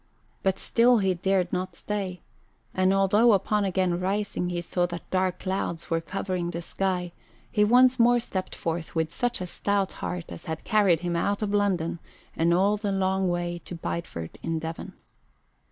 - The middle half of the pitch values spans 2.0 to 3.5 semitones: Yes, average, 2.7 semitones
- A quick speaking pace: No, average, 175 wpm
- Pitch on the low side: No, medium, 185 Hz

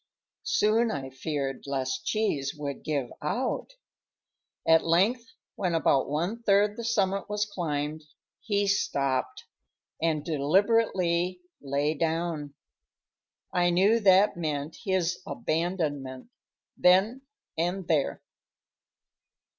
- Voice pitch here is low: No, medium, 170 Hz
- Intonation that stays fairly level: No, wide, 5.4 semitones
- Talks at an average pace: No, slow, 100 wpm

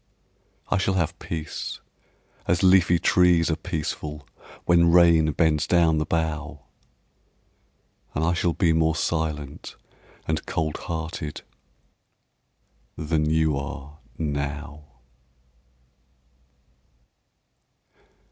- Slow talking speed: Yes, slow, 90 wpm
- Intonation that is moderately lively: No, narrow, 1.8 semitones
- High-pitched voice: No, very low, 80 Hz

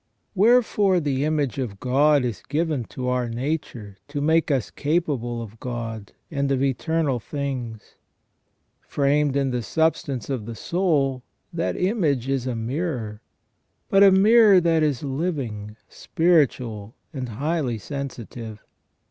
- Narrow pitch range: No, average, 5.1 semitones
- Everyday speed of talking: No, slow, 130 wpm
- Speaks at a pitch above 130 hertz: Yes, medium, 140 Hz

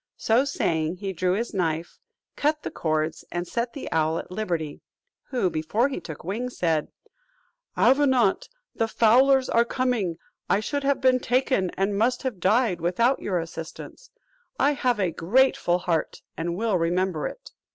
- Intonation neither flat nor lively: No, wide, 6.7 semitones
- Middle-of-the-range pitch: No, high, 200 Hz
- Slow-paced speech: No, average, 160 wpm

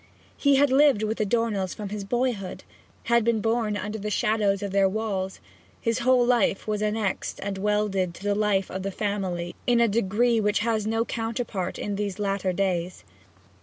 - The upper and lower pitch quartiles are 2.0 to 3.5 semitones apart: Yes, average, 2.7 semitones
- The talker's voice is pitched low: No, high, 210 Hz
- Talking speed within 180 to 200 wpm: Yes, average, 185 wpm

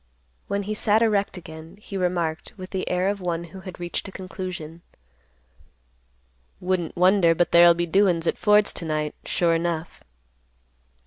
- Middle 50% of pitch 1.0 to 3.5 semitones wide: Yes, narrow, 2.4 semitones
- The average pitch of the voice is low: No, medium, 180 Hz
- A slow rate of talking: No, average, 155 wpm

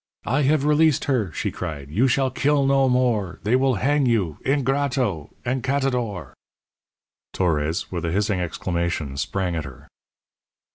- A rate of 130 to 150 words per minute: Yes, average, 140 wpm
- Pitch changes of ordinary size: No, wide, 7.8 semitones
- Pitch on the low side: Yes, low, 120 Hz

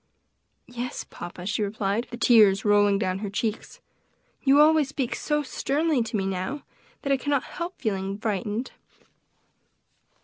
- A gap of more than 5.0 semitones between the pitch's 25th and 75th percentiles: Yes, wide, 5.5 semitones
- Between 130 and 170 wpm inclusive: Yes, average, 140 wpm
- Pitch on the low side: No, high, 225 Hz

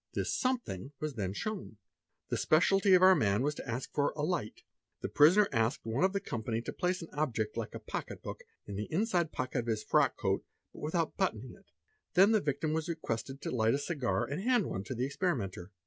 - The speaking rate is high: Yes, fast, 220 wpm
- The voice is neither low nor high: Yes, medium, 145 Hz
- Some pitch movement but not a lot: No, wide, 7.9 semitones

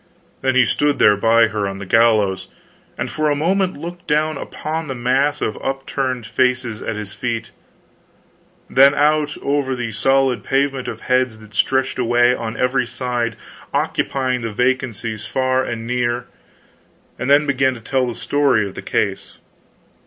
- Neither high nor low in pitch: No, low, 125 Hz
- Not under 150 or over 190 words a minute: Yes, average, 160 wpm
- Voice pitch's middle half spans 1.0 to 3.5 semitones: Yes, average, 3.1 semitones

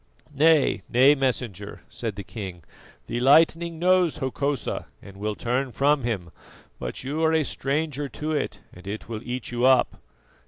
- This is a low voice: Yes, low, 130 Hz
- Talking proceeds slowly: No, average, 160 wpm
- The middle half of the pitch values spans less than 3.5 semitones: No, average, 4.9 semitones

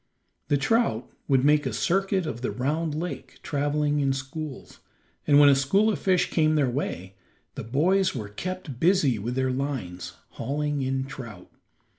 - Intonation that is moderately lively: Yes, average, 3.4 semitones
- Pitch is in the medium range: Yes, medium, 145 Hz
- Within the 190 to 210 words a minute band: No, average, 165 wpm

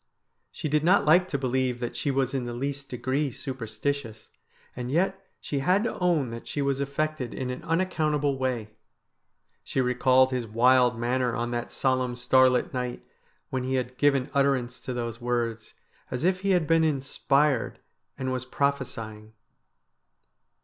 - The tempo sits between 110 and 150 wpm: No, average, 165 wpm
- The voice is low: Yes, low, 130 Hz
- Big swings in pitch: No, narrow, 2.6 semitones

